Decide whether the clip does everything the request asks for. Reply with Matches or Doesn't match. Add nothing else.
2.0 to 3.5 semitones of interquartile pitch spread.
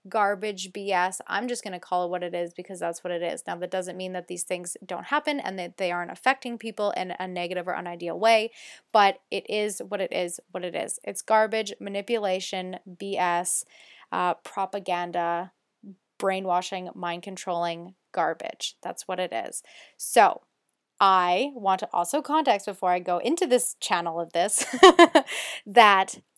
Matches